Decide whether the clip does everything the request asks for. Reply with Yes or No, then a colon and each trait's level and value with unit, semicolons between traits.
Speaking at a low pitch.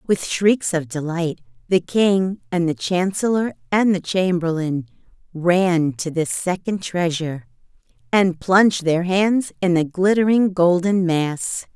No: medium, 180 Hz